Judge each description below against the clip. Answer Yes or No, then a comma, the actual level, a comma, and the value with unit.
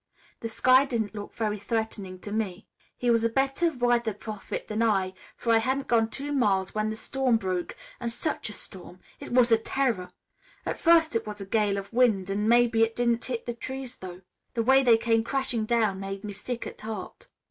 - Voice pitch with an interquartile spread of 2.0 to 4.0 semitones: Yes, average, 2.9 semitones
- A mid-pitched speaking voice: No, high, 225 Hz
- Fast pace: Yes, fast, 210 wpm